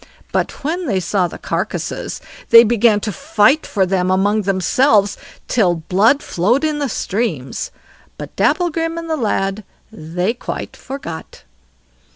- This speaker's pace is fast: No, slow, 135 wpm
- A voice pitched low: No, high, 215 Hz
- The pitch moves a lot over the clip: Yes, wide, 6.8 semitones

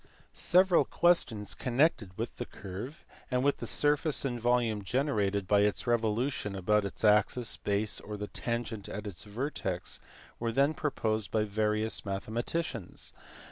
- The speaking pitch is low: Yes, low, 110 Hz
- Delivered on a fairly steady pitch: No, average, 3.8 semitones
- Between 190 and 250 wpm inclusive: No, average, 140 wpm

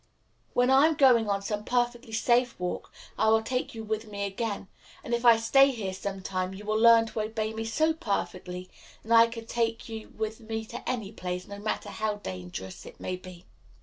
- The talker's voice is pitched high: Yes, high, 220 Hz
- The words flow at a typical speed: No, fast, 210 wpm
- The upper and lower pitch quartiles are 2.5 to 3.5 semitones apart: Yes, average, 2.8 semitones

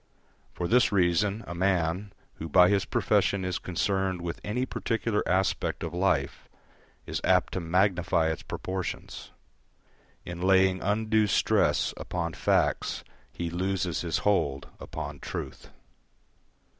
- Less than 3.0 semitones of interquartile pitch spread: Yes, narrow, 2.4 semitones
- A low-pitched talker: Yes, very low, 95 Hz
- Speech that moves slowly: Yes, slow, 125 wpm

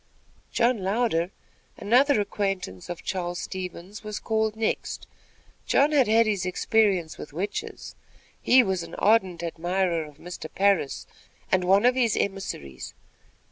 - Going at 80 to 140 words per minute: Yes, slow, 135 wpm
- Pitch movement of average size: Yes, average, 4.0 semitones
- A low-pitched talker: No, high, 195 Hz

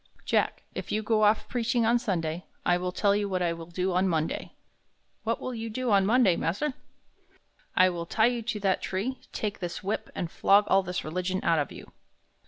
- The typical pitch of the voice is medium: No, high, 195 Hz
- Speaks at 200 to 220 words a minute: Yes, fast, 205 wpm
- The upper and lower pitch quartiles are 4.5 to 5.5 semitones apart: No, average, 3.9 semitones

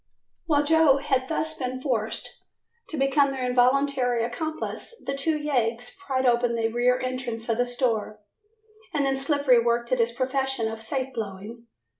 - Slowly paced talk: No, average, 160 wpm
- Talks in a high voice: Yes, very high, 255 Hz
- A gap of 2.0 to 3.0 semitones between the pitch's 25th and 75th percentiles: Yes, average, 2.7 semitones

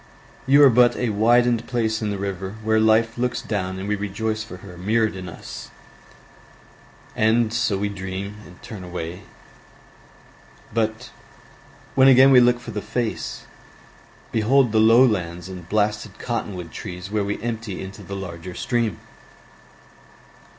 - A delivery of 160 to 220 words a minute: No, average, 150 wpm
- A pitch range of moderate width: Yes, average, 3.4 semitones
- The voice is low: Yes, low, 110 Hz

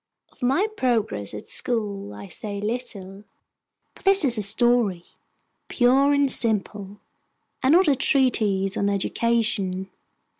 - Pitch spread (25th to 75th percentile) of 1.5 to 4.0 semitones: No, average, 4.6 semitones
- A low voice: No, high, 220 Hz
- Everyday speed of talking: No, slow, 125 wpm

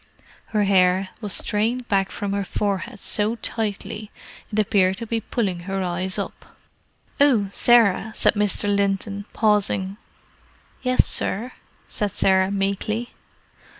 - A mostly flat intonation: Yes, narrow, 2.1 semitones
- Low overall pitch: No, high, 200 Hz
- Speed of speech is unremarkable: No, slow, 125 wpm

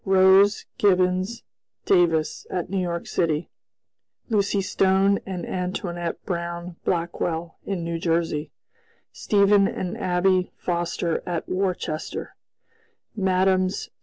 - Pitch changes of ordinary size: No, narrow, 1.9 semitones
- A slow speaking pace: Yes, slow, 100 wpm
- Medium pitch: Yes, medium, 180 Hz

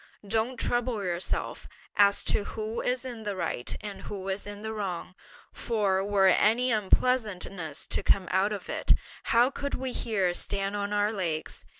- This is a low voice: No, high, 205 Hz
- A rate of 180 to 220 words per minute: No, average, 170 wpm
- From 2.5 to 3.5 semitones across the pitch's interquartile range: Yes, average, 2.8 semitones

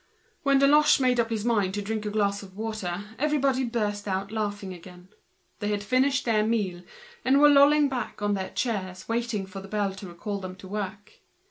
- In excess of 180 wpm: Yes, average, 195 wpm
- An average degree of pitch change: Yes, average, 3.9 semitones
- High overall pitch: Yes, high, 210 Hz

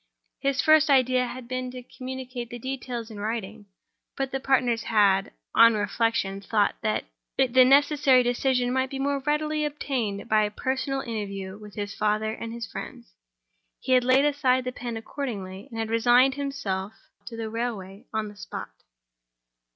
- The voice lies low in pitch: No, high, 245 Hz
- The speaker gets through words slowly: No, average, 165 wpm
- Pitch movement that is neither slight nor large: Yes, average, 3.5 semitones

